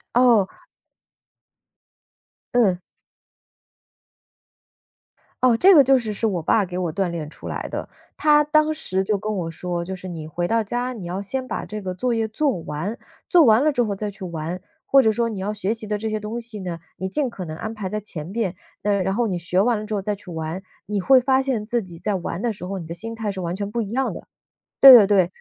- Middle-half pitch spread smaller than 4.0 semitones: No, average, 4.3 semitones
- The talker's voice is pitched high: Yes, high, 210 Hz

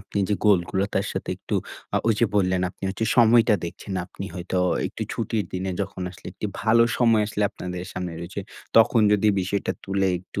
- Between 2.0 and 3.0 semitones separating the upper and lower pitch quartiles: Yes, average, 2.7 semitones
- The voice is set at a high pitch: No, low, 100 Hz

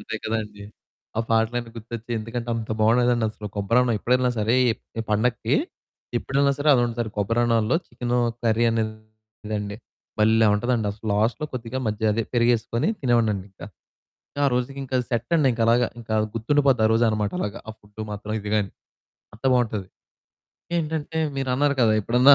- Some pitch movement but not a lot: No, narrow, 2.2 semitones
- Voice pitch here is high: No, low, 115 Hz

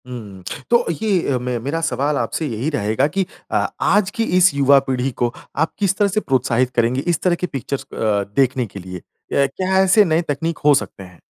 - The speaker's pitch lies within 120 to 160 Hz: Yes, medium, 140 Hz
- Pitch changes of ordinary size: No, wide, 5.9 semitones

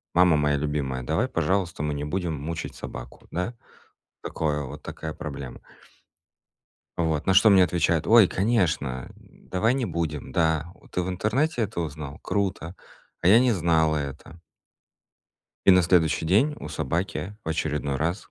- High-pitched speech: No, very low, 85 Hz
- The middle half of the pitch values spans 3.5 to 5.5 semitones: Yes, average, 4.1 semitones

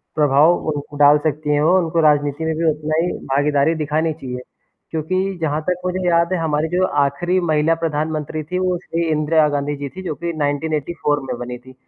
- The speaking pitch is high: No, medium, 155 Hz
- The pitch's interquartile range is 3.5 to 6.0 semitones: No, narrow, 2.4 semitones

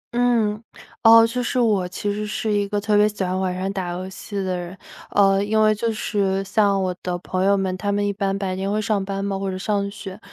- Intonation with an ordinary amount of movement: No, narrow, 1.8 semitones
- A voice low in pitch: No, high, 200 Hz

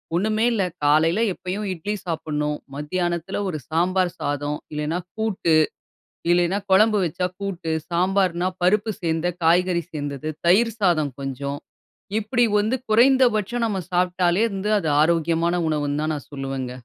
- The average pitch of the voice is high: No, medium, 175 Hz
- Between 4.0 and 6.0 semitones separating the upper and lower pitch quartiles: Yes, average, 4.4 semitones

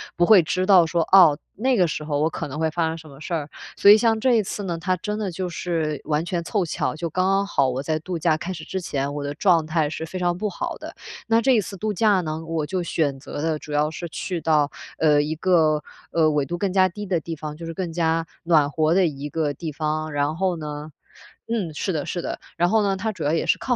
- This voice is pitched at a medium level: Yes, medium, 165 Hz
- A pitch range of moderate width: Yes, average, 3.4 semitones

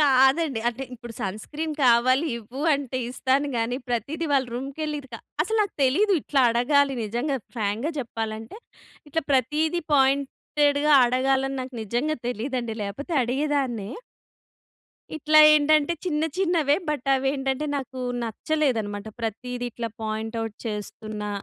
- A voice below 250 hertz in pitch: No, very high, 265 Hz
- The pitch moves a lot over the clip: No, average, 4.1 semitones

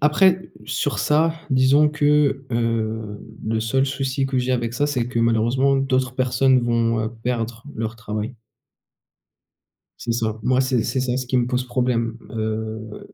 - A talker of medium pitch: No, low, 125 Hz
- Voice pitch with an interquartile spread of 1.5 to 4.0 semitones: Yes, average, 2.8 semitones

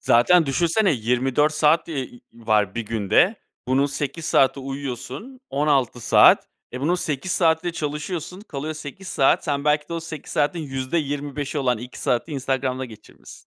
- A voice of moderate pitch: Yes, medium, 145 Hz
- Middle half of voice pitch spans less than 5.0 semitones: Yes, average, 3.5 semitones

